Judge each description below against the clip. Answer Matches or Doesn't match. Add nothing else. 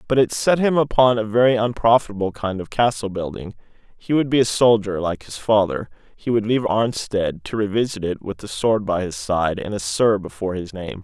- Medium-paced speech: Doesn't match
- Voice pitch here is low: Matches